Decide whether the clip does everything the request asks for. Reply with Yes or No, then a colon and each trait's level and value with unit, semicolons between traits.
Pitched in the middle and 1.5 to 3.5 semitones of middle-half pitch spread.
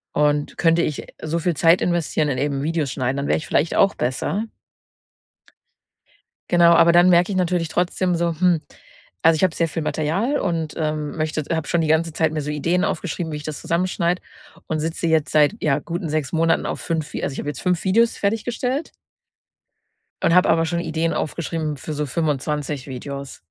Yes: medium, 165 Hz; narrow, 2.4 semitones